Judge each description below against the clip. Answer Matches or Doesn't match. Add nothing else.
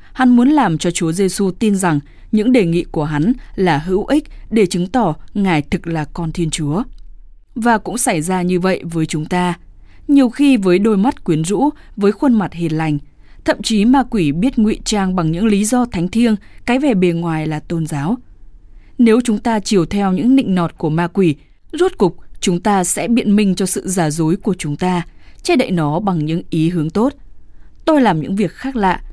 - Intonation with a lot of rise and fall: Matches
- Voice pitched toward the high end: Matches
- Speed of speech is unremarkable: Doesn't match